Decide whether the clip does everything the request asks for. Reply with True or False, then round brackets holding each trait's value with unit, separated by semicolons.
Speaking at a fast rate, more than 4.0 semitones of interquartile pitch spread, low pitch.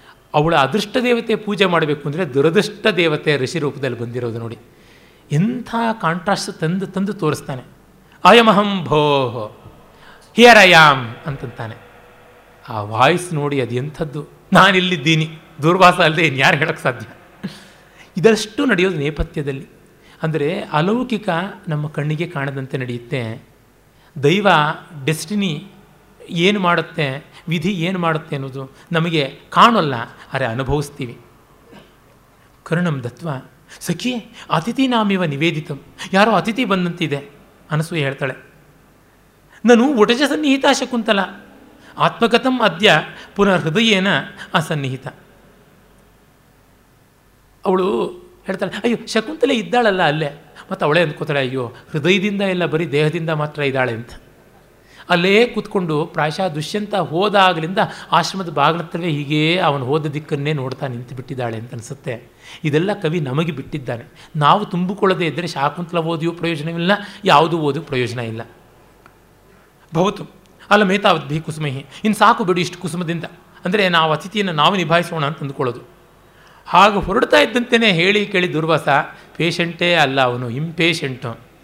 False (110 wpm; 5.2 semitones; 165 Hz)